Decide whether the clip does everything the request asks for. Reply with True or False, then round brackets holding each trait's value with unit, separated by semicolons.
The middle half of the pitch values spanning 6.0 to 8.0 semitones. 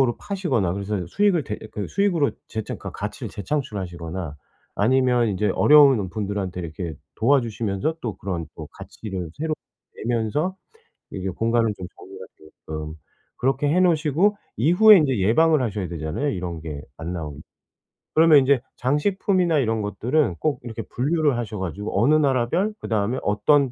True (7.6 semitones)